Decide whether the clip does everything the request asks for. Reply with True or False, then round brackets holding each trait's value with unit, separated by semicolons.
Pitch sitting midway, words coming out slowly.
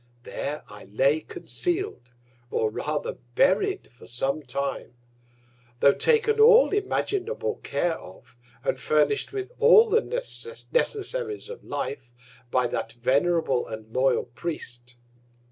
True (155 Hz; 115 wpm)